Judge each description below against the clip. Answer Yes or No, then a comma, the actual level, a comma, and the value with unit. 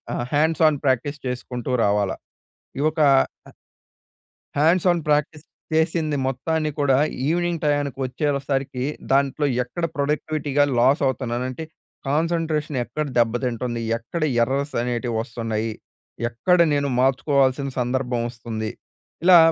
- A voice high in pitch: No, medium, 140 Hz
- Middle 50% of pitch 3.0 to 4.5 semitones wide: Yes, average, 3.8 semitones